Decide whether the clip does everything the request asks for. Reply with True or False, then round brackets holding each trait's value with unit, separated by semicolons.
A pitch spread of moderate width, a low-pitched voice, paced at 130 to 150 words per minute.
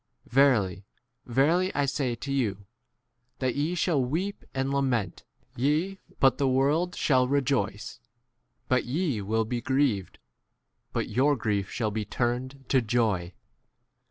True (4.1 semitones; 130 Hz; 140 wpm)